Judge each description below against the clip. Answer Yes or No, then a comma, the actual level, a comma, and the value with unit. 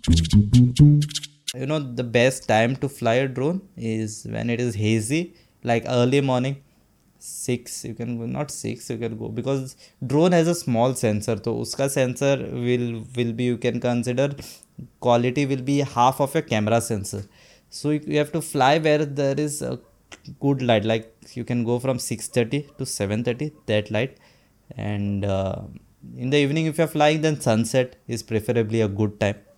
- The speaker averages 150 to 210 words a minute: Yes, average, 175 wpm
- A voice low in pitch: Yes, low, 125 Hz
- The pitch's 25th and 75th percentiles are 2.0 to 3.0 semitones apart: No, average, 3.8 semitones